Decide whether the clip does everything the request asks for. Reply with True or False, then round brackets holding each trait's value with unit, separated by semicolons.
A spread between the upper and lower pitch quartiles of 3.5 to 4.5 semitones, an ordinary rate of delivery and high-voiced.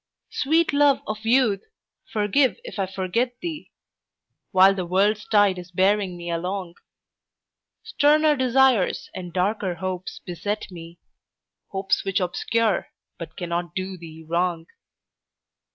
False (4.2 semitones; 120 wpm; 195 Hz)